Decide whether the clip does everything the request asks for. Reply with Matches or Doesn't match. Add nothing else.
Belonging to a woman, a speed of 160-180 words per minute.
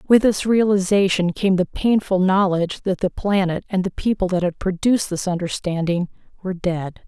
Matches